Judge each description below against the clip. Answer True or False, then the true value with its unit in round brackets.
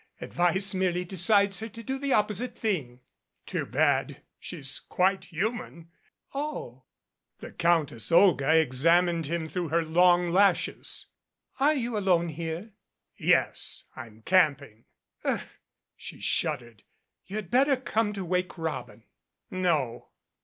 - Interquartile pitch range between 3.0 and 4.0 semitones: False (4.5 semitones)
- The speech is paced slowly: True (125 wpm)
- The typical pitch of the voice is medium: True (175 Hz)